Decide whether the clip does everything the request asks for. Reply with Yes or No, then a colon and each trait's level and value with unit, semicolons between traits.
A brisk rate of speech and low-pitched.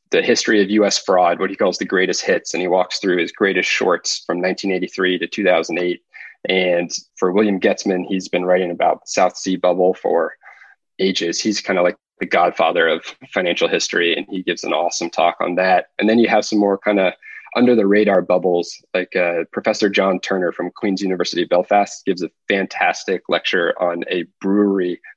No: average, 190 wpm; very low, 95 Hz